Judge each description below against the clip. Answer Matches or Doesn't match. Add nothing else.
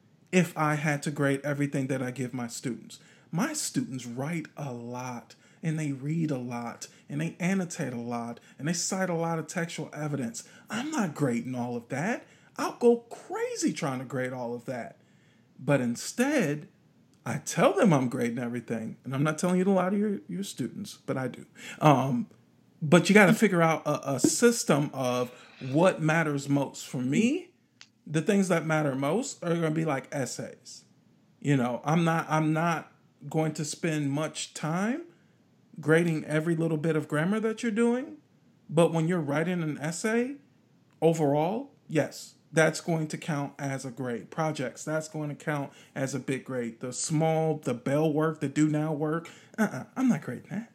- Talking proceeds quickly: Doesn't match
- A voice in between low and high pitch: Matches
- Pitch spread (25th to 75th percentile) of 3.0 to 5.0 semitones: Matches